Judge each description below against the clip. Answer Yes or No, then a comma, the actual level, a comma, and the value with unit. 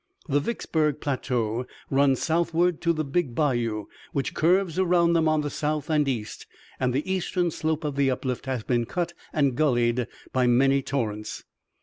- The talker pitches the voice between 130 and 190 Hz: Yes, medium, 140 Hz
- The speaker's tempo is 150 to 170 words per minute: Yes, average, 165 wpm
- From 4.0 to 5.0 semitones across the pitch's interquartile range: Yes, average, 4.3 semitones